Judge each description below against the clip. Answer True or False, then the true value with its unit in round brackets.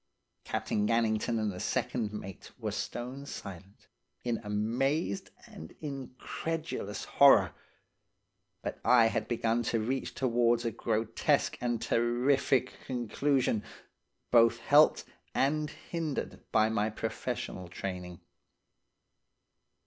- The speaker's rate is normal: False (105 wpm)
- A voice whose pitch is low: True (115 Hz)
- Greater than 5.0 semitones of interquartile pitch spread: False (3.8 semitones)